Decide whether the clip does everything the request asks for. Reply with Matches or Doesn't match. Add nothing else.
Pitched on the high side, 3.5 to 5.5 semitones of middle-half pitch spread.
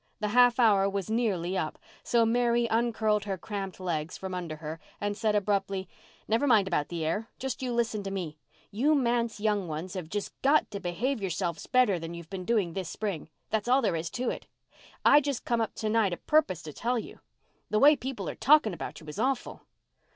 Matches